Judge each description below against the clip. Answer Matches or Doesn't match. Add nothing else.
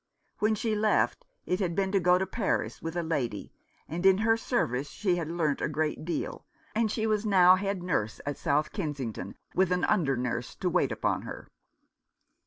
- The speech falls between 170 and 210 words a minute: Matches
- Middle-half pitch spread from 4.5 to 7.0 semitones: Matches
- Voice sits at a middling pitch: Matches